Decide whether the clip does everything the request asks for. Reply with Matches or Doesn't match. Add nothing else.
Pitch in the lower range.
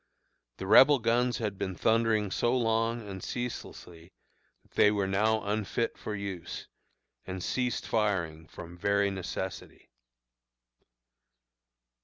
Matches